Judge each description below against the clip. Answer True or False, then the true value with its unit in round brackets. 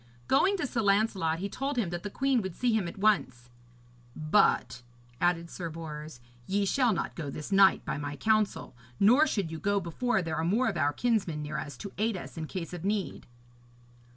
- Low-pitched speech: False (190 Hz)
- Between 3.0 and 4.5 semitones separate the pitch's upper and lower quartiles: False (5.3 semitones)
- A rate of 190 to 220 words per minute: True (205 wpm)